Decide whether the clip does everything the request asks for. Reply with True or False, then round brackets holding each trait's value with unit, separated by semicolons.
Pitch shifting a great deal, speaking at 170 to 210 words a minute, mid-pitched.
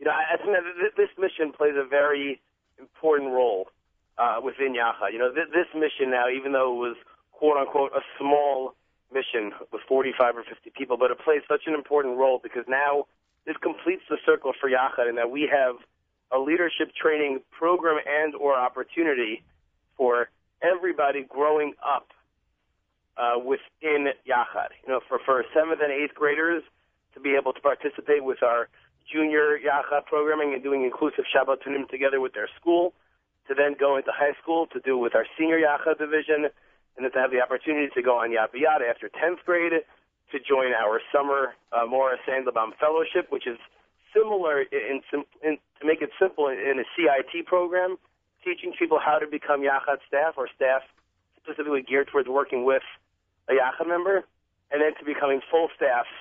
False (3.2 semitones; 175 wpm; 145 Hz)